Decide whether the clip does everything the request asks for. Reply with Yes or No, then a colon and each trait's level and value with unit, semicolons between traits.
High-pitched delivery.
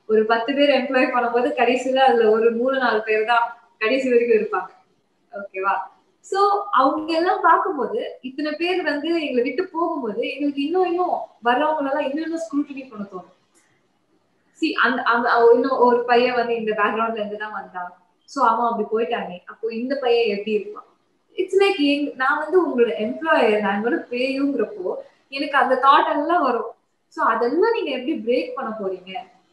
Yes: very high, 255 Hz